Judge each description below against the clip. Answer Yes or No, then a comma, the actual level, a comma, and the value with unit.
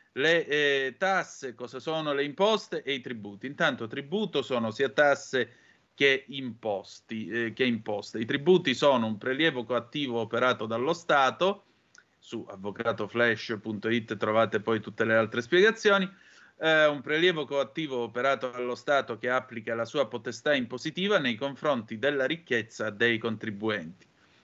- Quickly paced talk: No, average, 140 wpm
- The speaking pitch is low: Yes, low, 125 Hz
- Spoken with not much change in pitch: No, average, 4.2 semitones